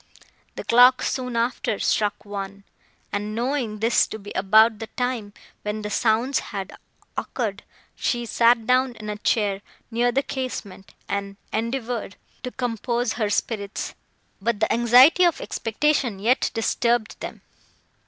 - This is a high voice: Yes, high, 230 Hz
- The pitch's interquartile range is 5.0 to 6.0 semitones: No, average, 2.9 semitones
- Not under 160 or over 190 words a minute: No, average, 140 wpm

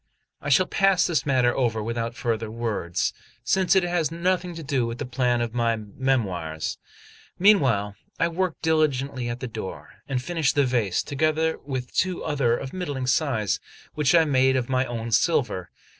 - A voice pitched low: Yes, low, 130 Hz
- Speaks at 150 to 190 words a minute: Yes, average, 175 wpm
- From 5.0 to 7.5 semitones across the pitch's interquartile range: Yes, wide, 5.4 semitones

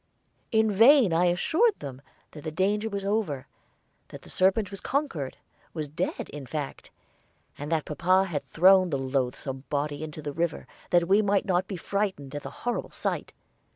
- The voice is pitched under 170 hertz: No, medium, 175 Hz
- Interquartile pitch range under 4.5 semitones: No, wide, 5.4 semitones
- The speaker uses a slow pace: No, average, 175 wpm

